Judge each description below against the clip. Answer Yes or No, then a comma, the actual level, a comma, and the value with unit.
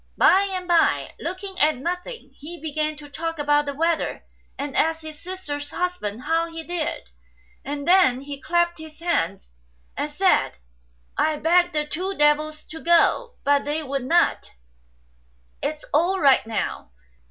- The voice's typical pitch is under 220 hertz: No, very high, 315 Hz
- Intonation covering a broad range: No, average, 3.1 semitones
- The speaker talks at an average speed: Yes, average, 155 wpm